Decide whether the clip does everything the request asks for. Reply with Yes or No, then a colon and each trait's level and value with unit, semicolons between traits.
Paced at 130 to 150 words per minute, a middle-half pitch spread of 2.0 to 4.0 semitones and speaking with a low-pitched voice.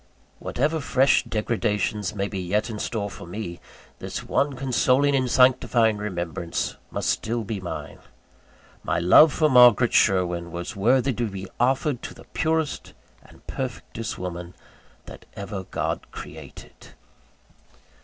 No: slow, 135 wpm; average, 5.3 semitones; low, 110 Hz